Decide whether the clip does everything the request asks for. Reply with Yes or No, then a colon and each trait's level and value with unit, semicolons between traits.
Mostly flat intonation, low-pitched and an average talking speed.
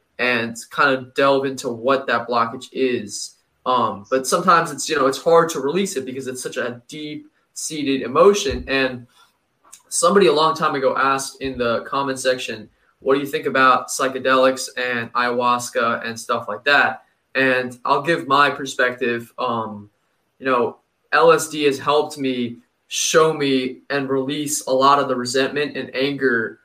Yes: narrow, 2.3 semitones; low, 130 Hz; average, 165 wpm